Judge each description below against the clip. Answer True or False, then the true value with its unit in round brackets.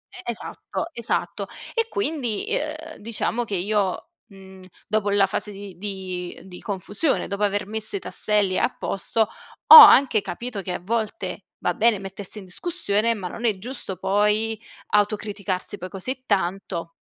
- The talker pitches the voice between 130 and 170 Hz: False (205 Hz)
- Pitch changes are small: False (3.1 semitones)